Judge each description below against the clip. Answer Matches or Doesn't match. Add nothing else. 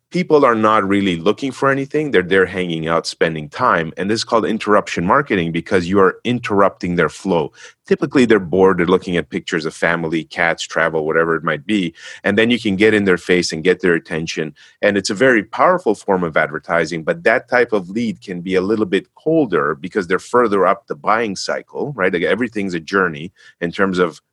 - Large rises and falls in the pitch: Doesn't match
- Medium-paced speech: Doesn't match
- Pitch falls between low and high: Doesn't match